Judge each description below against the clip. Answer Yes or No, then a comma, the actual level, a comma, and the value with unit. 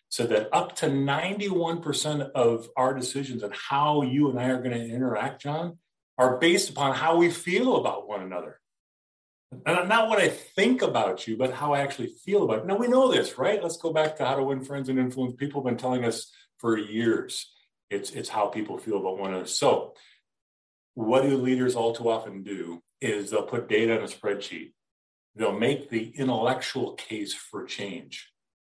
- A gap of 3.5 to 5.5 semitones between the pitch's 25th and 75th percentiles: Yes, average, 4.2 semitones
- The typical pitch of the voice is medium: No, low, 130 Hz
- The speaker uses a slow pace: No, average, 195 wpm